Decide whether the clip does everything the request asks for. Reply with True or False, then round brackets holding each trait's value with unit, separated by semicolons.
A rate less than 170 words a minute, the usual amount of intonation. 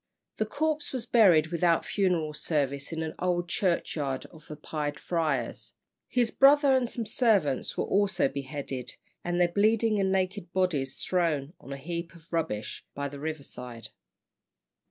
False (155 wpm; 5.7 semitones)